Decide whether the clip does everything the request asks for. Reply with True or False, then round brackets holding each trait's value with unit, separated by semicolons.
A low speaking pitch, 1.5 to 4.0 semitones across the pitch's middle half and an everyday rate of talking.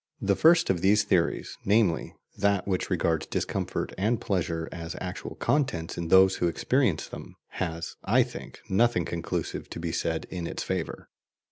True (90 Hz; 3.5 semitones; 160 wpm)